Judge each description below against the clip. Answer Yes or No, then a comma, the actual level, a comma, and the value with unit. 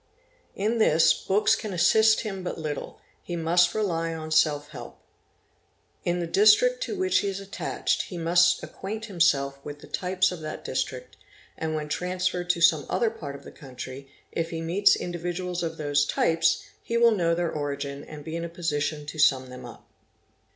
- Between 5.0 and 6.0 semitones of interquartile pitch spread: No, average, 3.9 semitones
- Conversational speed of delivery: Yes, average, 180 wpm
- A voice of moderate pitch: Yes, medium, 170 Hz